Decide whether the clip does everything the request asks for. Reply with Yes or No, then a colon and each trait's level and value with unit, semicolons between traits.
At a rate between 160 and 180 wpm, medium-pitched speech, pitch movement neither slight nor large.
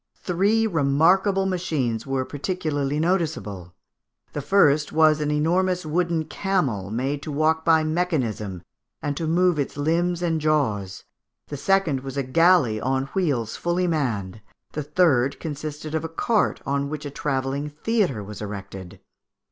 No: average, 145 wpm; medium, 150 Hz; average, 4.4 semitones